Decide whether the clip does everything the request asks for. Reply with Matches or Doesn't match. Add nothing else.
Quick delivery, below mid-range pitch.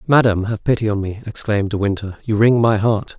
Matches